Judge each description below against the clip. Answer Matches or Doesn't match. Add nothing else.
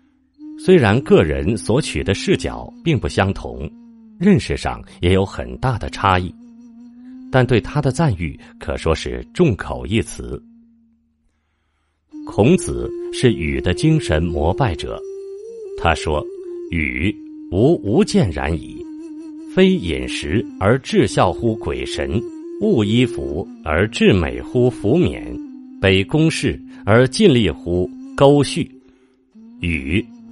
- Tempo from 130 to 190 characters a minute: Matches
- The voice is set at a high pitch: Doesn't match